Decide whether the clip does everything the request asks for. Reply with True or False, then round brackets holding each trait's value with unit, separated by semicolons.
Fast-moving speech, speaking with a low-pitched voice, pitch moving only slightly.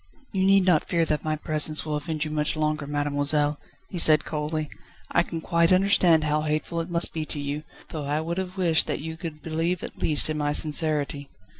False (210 wpm; 155 Hz; 1.9 semitones)